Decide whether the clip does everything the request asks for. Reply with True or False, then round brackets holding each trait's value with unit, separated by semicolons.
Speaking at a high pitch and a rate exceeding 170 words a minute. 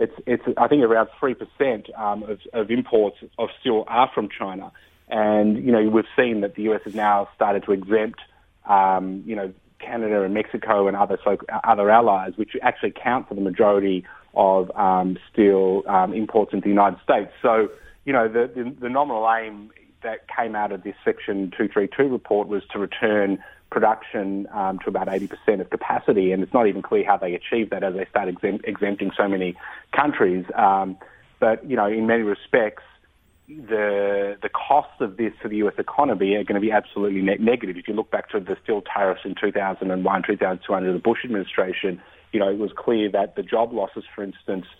False (105 Hz; 200 wpm)